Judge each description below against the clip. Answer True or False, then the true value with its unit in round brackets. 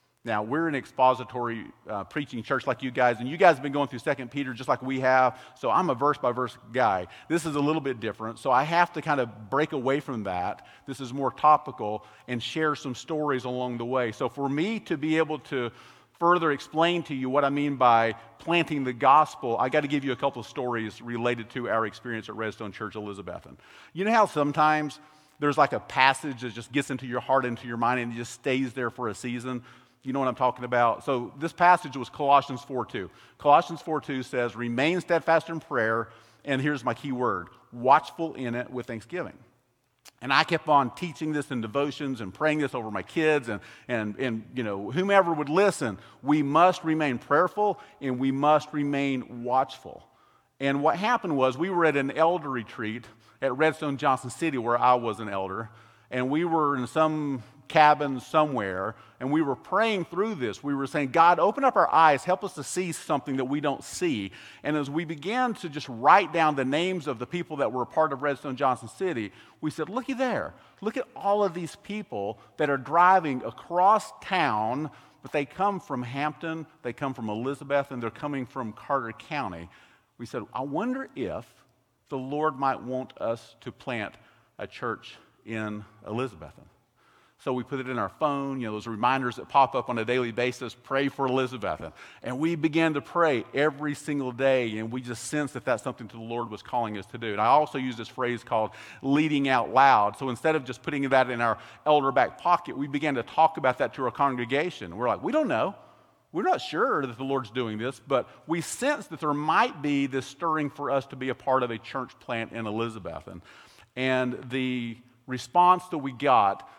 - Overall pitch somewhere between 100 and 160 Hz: True (135 Hz)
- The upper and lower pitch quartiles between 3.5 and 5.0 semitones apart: True (3.9 semitones)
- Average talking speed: False (210 wpm)